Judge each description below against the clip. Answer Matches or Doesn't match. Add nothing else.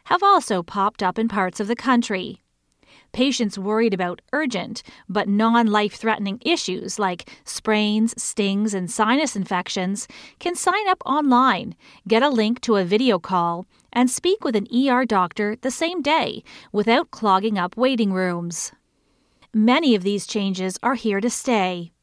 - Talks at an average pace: Matches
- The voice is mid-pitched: Doesn't match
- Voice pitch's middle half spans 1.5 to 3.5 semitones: Doesn't match